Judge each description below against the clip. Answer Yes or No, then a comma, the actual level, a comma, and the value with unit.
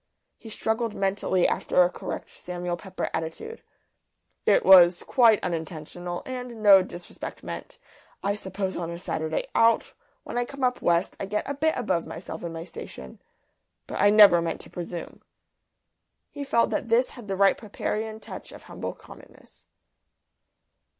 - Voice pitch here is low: No, high, 195 Hz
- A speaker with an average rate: Yes, average, 155 wpm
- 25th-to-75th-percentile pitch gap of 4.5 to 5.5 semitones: Yes, average, 4.8 semitones